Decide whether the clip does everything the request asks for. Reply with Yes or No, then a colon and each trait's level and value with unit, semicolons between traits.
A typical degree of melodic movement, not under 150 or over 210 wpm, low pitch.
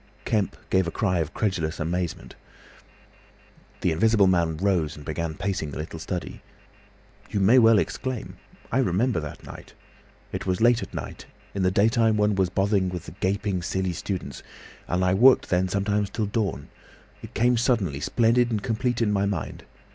Yes: average, 3.8 semitones; average, 165 wpm; low, 100 Hz